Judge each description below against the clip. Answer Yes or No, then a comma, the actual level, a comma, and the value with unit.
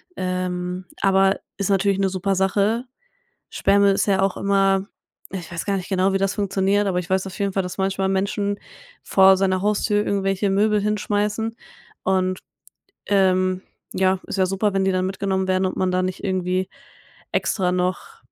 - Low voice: No, high, 195 Hz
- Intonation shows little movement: Yes, narrow, 1.2 semitones